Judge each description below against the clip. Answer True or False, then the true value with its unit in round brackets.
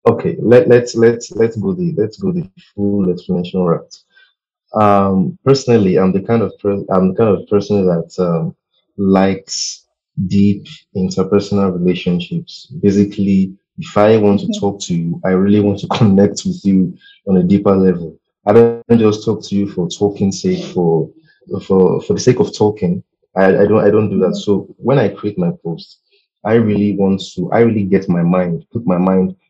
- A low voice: True (100 Hz)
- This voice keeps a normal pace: True (185 wpm)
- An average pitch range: True (3.9 semitones)